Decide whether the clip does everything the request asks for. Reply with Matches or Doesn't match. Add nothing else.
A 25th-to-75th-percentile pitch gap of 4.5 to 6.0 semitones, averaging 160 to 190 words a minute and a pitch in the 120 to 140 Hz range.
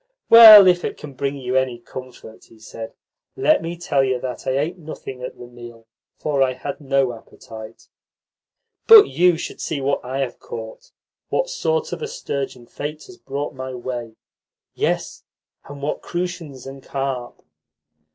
Matches